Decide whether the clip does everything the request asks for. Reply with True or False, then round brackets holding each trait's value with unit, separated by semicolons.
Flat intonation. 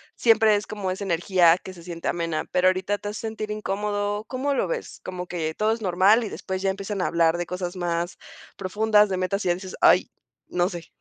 False (3.1 semitones)